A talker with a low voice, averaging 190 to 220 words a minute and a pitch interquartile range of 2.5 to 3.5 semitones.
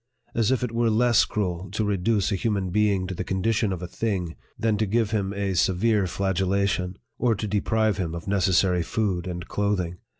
Yes: low, 100 Hz; average, 200 wpm; average, 3.0 semitones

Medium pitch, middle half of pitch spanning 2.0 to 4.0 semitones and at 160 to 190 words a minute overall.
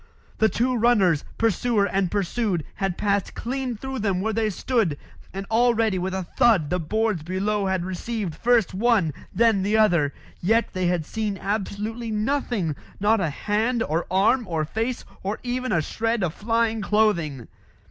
No: high, 210 Hz; average, 3.7 semitones; average, 165 wpm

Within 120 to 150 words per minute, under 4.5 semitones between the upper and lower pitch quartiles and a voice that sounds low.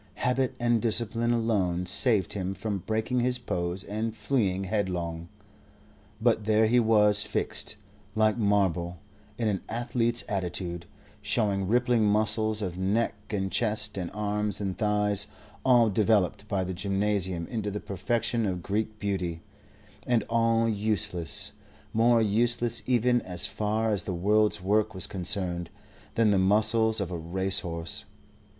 Yes: average, 140 wpm; average, 3.2 semitones; low, 105 Hz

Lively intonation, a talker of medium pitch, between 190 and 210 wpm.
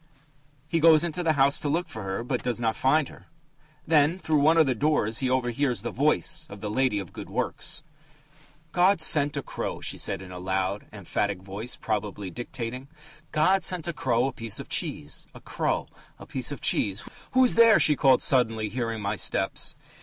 No: wide, 6.4 semitones; low, 125 Hz; average, 200 wpm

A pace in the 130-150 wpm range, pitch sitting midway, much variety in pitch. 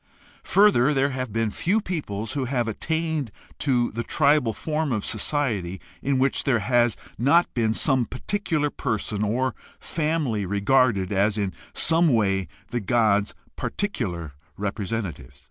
No: average, 140 wpm; low, 120 Hz; wide, 5.9 semitones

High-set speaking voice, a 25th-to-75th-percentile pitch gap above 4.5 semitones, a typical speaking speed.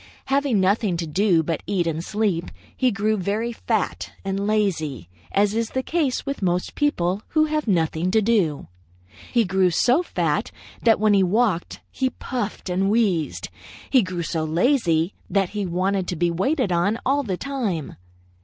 Yes: high, 200 Hz; average, 5.0 semitones; average, 170 wpm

